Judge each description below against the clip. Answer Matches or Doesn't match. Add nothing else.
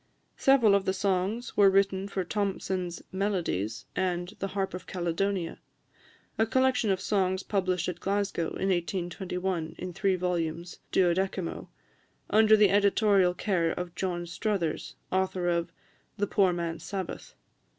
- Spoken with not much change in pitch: Matches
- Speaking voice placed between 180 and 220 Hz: Matches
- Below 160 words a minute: Matches